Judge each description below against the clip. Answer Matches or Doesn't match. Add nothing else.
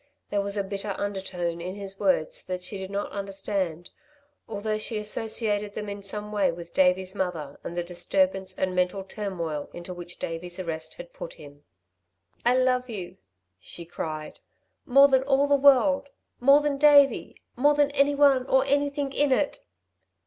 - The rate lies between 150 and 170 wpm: Matches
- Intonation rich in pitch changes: Matches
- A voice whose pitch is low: Doesn't match